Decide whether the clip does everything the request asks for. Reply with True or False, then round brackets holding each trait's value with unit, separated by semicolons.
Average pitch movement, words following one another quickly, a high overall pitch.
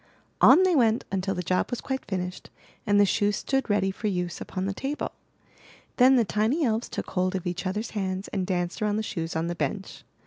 True (3.4 semitones; 215 wpm; 195 Hz)